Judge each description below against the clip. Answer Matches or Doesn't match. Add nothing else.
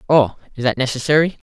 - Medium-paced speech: Matches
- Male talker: Matches